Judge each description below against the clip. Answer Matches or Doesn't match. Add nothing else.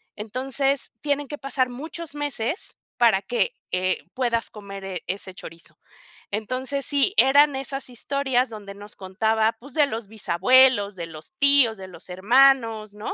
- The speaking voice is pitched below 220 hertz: Doesn't match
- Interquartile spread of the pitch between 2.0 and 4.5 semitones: Doesn't match